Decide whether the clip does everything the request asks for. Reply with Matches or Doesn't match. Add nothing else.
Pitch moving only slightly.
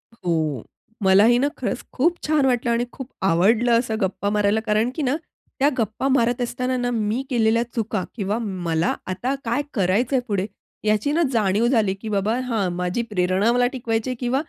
Doesn't match